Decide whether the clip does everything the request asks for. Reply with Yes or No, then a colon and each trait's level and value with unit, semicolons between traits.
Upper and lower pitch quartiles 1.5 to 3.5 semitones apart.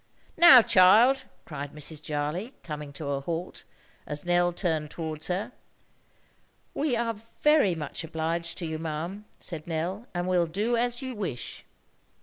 No: average, 5.3 semitones